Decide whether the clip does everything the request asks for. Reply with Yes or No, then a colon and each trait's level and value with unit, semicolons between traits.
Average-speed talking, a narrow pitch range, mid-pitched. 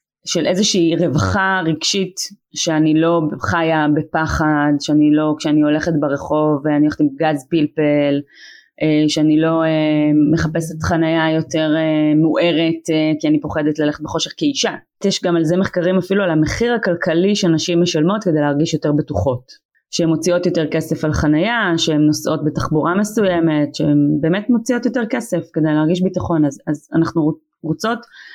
Yes: average, 140 wpm; narrow, 2.3 semitones; medium, 160 Hz